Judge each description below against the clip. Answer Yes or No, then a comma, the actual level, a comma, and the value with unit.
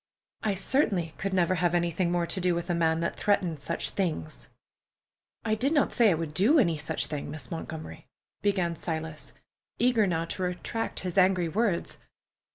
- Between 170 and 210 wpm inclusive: Yes, average, 175 wpm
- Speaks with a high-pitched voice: No, medium, 175 Hz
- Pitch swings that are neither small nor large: Yes, average, 3.3 semitones